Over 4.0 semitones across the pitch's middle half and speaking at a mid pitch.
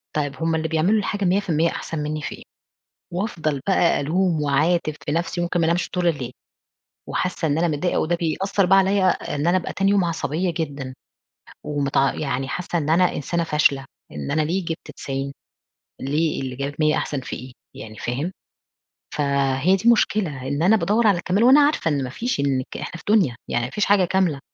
Yes: average, 4.5 semitones; medium, 160 Hz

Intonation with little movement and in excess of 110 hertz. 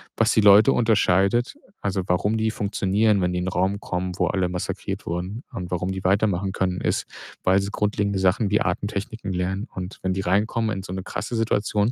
No: narrow, 2.3 semitones; low, 100 Hz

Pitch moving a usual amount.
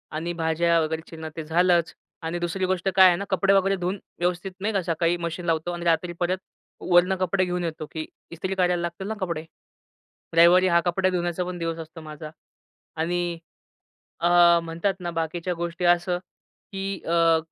No: narrow, 1.7 semitones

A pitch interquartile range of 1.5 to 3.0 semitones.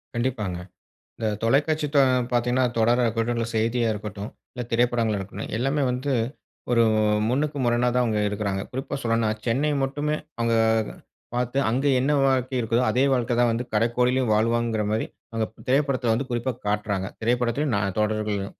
Yes: narrow, 2.6 semitones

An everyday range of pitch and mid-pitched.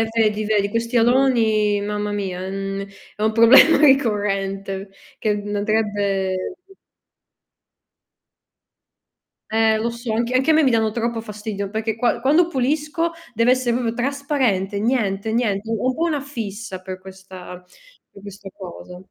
No: average, 3.4 semitones; high, 220 Hz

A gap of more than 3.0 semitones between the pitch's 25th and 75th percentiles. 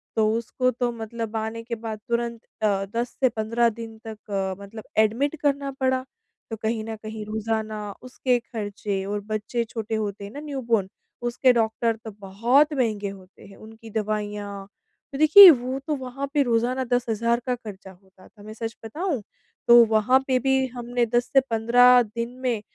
No: narrow, 2.5 semitones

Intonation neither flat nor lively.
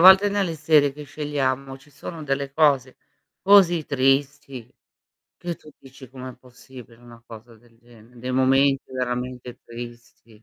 Yes: average, 3.0 semitones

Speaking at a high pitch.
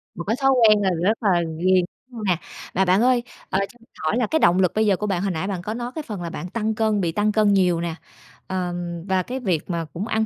Yes: high, 195 Hz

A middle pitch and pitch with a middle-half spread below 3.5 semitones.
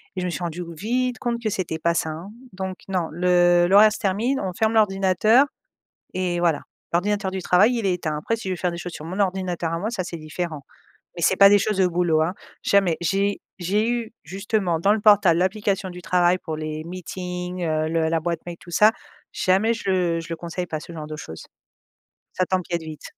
Yes: medium, 180 Hz; average, 2.9 semitones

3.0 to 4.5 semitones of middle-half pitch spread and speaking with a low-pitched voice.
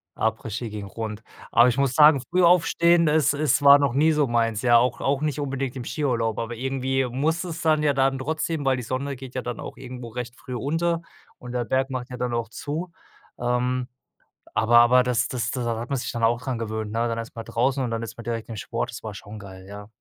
Yes: average, 3.3 semitones; low, 125 Hz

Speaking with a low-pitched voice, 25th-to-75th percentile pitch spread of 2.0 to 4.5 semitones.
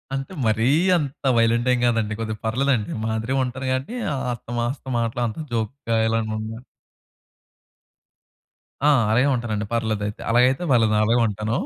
Yes: low, 115 Hz; narrow, 2.5 semitones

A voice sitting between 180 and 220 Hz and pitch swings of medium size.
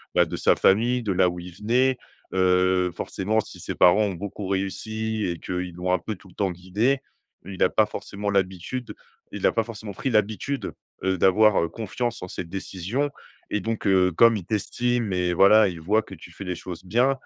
No: low, 100 Hz; average, 3.3 semitones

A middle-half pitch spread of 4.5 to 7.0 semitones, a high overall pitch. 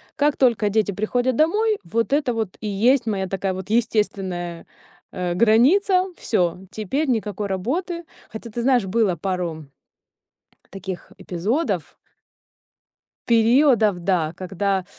Yes: average, 4.9 semitones; high, 215 Hz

